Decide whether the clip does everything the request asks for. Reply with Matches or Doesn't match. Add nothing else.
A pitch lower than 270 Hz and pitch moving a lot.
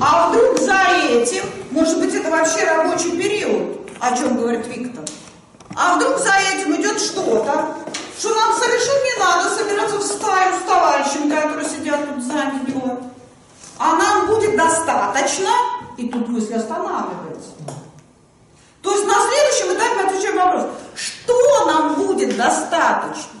Doesn't match